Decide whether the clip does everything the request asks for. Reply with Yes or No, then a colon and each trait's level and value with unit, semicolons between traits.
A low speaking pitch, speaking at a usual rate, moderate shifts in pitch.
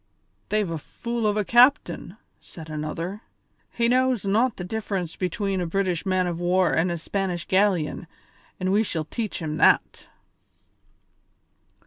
No: high, 190 Hz; average, 145 wpm; average, 3.7 semitones